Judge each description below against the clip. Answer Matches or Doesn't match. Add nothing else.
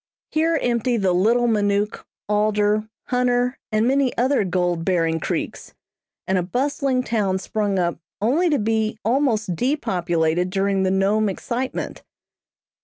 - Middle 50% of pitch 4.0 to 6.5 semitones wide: Matches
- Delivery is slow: Matches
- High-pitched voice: Matches